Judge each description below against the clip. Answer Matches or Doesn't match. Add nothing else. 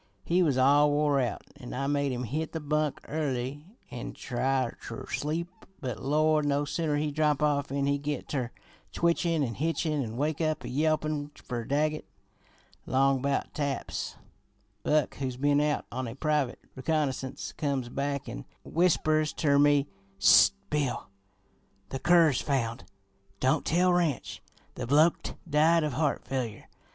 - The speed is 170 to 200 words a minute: Doesn't match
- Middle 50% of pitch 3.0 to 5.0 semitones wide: Doesn't match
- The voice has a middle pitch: Matches